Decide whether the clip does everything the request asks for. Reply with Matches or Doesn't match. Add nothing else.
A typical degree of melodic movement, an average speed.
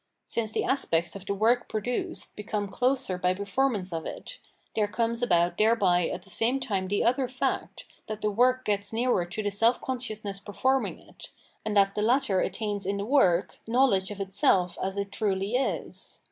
Matches